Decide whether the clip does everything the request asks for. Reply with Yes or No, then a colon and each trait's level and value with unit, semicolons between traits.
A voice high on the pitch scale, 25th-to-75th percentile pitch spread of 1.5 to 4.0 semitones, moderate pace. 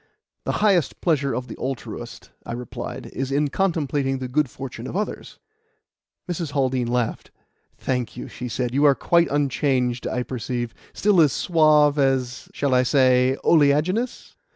No: low, 135 Hz; average, 3.2 semitones; average, 155 wpm